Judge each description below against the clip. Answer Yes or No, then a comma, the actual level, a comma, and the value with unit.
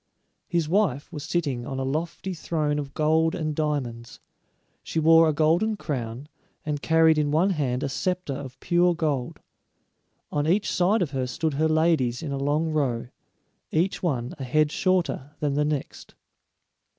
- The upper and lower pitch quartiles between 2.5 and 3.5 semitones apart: Yes, average, 3.0 semitones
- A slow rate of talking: No, average, 165 wpm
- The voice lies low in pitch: No, medium, 155 Hz